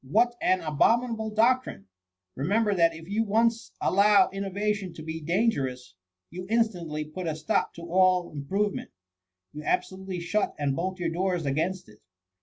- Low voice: No, medium, 185 Hz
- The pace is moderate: Yes, average, 165 wpm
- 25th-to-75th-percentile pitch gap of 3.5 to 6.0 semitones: Yes, average, 5.0 semitones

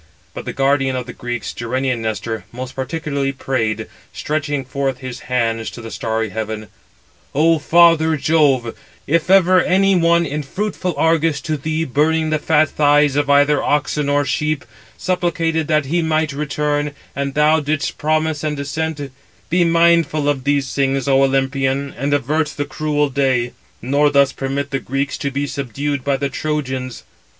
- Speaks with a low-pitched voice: No, medium, 145 Hz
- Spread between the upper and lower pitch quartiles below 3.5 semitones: Yes, average, 2.7 semitones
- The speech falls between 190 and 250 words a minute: No, average, 160 wpm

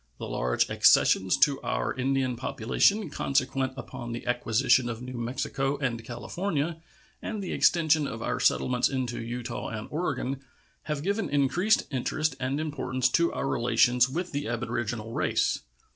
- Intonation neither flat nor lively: Yes, average, 3.5 semitones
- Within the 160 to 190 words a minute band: No, average, 145 wpm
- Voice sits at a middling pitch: No, low, 130 Hz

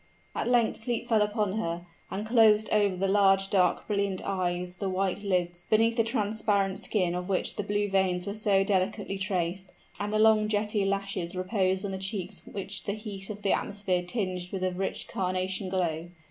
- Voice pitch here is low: No, high, 195 Hz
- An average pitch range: No, narrow, 2.1 semitones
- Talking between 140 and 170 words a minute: No, average, 190 wpm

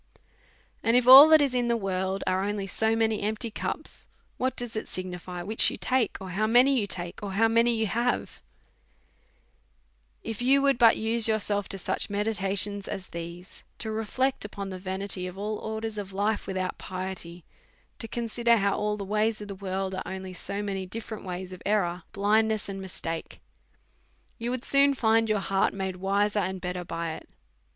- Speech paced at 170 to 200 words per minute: Yes, average, 185 wpm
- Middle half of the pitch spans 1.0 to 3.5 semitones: Yes, average, 2.9 semitones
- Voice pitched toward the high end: Yes, high, 205 Hz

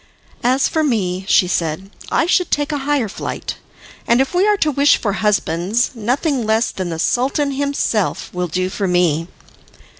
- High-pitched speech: Yes, high, 230 Hz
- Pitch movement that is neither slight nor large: No, wide, 7.4 semitones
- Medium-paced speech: Yes, average, 175 wpm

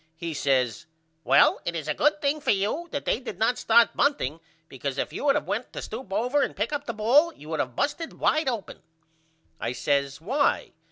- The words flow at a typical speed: No, fast, 215 wpm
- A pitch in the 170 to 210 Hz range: No, high, 220 Hz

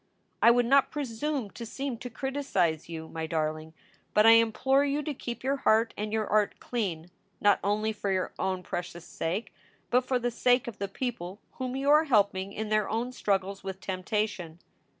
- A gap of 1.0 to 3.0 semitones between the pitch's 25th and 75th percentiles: No, average, 4.8 semitones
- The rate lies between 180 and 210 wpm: Yes, average, 190 wpm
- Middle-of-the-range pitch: No, high, 215 Hz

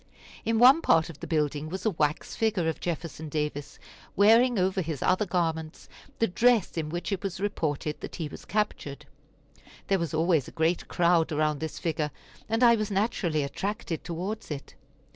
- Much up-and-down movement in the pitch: No, average, 4.8 semitones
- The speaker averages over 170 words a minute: Yes, average, 180 wpm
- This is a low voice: No, medium, 170 Hz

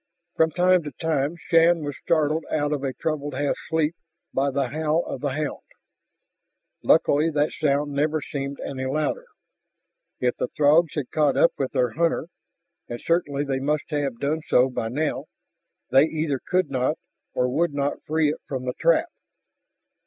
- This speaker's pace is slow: No, average, 165 wpm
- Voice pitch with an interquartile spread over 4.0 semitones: No, narrow, 2.5 semitones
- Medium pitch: Yes, medium, 145 Hz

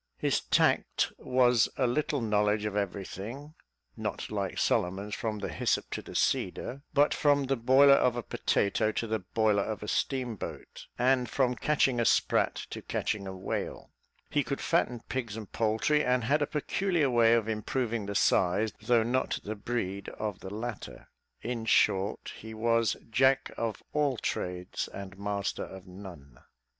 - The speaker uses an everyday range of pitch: Yes, average, 3.8 semitones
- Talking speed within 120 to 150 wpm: No, average, 165 wpm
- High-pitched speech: No, low, 115 Hz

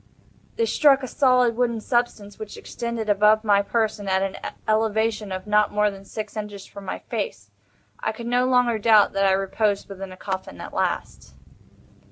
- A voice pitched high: Yes, high, 215 Hz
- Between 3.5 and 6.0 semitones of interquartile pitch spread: No, average, 2.8 semitones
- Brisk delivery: No, average, 180 wpm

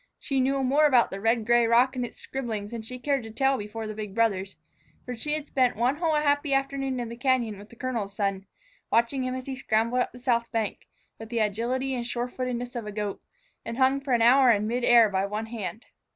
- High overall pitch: Yes, high, 240 Hz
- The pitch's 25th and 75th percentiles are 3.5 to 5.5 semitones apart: No, average, 2.9 semitones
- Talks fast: Yes, fast, 240 wpm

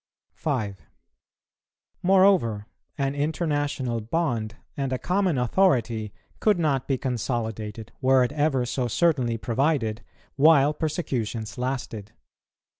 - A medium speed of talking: No, slow, 105 wpm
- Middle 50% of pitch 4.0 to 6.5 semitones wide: Yes, average, 5.0 semitones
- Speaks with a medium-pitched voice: No, low, 130 Hz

